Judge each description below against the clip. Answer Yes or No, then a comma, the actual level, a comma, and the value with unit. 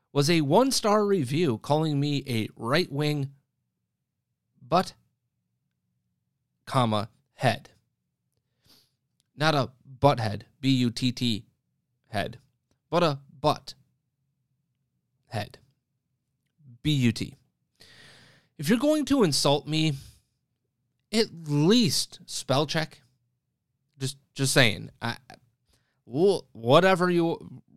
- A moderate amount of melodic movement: Yes, average, 3.4 semitones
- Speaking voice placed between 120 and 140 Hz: Yes, low, 135 Hz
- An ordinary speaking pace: No, slow, 90 wpm